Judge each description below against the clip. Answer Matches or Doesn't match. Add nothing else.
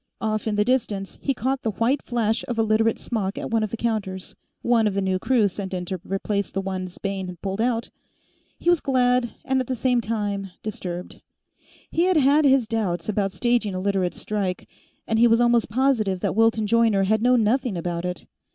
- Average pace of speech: Doesn't match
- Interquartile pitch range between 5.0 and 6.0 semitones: Doesn't match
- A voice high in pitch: Matches